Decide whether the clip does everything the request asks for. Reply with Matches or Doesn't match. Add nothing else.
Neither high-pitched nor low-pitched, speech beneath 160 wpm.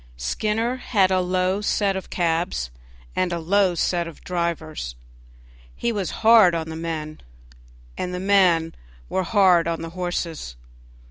Matches